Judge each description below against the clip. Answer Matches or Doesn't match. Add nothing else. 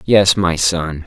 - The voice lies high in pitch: Doesn't match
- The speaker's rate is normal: Matches